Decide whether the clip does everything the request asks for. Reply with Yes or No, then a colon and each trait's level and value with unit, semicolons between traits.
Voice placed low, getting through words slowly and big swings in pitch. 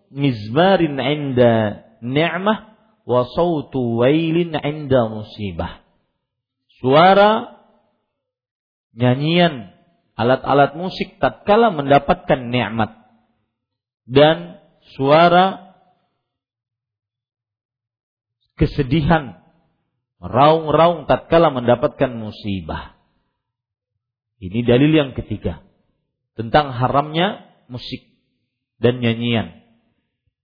Yes: low, 130 Hz; slow, 55 wpm; wide, 5.9 semitones